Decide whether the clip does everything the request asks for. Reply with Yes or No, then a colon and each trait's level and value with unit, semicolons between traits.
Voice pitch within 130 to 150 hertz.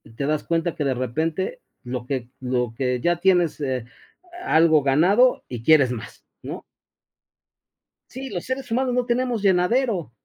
No: medium, 160 Hz